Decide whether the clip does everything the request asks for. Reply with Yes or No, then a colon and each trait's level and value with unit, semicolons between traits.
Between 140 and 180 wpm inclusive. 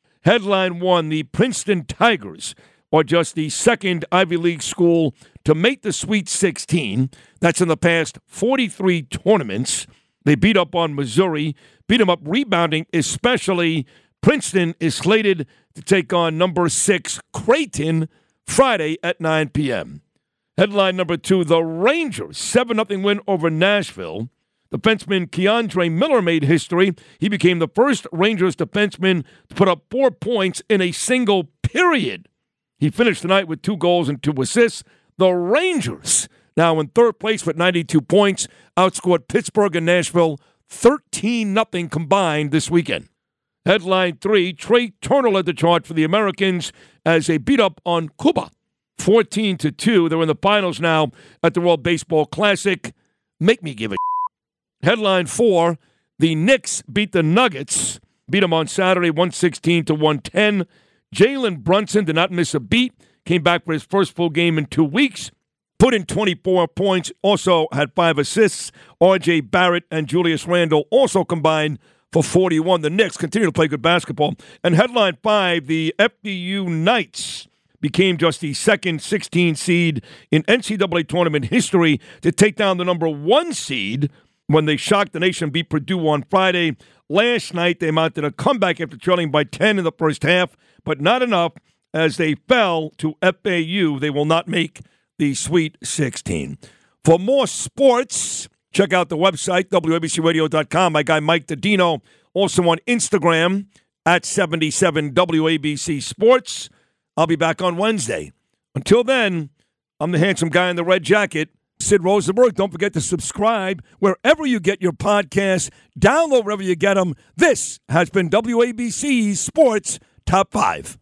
Yes: average, 155 wpm